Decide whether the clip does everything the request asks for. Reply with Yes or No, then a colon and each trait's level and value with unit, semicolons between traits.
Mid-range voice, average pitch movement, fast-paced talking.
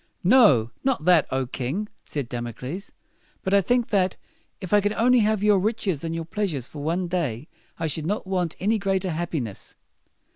No: medium, 180 Hz; wide, 5.7 semitones; fast, 210 wpm